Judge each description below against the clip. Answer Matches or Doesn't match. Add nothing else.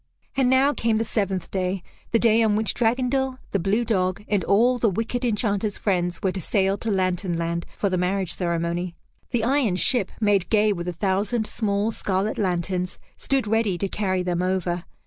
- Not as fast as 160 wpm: Doesn't match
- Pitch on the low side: Doesn't match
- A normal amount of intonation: Matches